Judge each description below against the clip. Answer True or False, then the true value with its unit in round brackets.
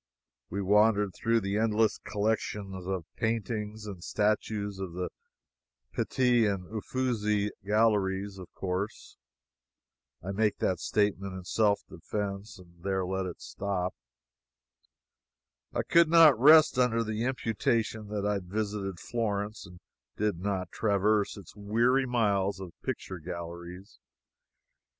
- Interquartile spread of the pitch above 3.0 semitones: False (2.5 semitones)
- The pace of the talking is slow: True (120 wpm)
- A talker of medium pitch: False (105 Hz)